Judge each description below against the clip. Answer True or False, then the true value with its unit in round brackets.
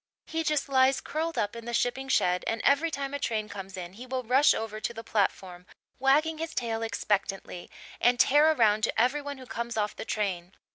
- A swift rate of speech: True (210 wpm)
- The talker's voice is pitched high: True (235 Hz)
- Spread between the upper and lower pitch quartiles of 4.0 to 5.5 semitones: True (5.0 semitones)